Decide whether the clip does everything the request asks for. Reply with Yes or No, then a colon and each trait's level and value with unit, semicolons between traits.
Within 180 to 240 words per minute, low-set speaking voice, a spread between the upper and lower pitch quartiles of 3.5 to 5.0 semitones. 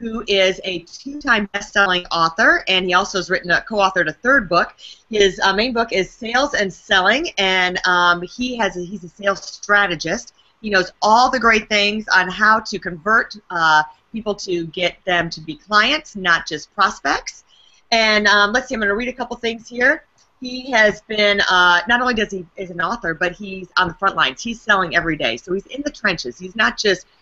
No: fast, 205 wpm; high, 200 Hz; average, 3.8 semitones